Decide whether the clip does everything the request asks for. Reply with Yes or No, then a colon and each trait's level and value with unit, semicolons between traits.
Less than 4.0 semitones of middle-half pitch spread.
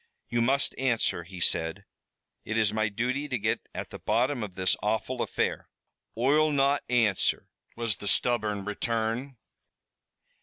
Yes: average, 3.6 semitones